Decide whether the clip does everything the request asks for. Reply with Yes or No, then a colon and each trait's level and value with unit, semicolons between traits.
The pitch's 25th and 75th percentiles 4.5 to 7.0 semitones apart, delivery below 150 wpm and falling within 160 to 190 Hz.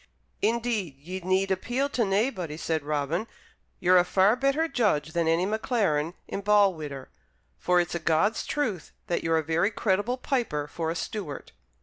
No: average, 5.2 semitones; average, 160 wpm; medium, 185 Hz